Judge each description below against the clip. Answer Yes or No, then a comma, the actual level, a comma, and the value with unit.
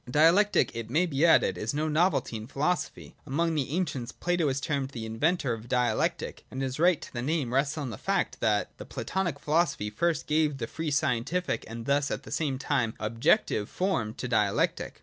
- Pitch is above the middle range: No, medium, 140 Hz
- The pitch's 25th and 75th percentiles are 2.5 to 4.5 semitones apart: No, average, 5.3 semitones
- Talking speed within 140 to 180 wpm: No, average, 200 wpm